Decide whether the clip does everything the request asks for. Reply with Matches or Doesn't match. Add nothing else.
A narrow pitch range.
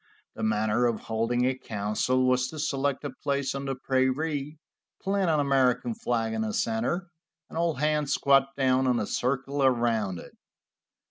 Doesn't match